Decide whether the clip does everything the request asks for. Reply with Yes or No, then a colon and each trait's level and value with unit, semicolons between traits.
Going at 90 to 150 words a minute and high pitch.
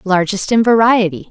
Yes: average, 140 wpm; high, 205 Hz